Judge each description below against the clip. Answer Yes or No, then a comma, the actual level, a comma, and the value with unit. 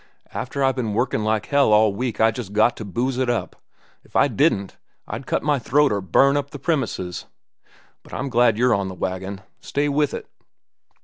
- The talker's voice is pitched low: Yes, low, 120 Hz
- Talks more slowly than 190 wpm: No, average, 195 wpm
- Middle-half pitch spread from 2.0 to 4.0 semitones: No, average, 4.8 semitones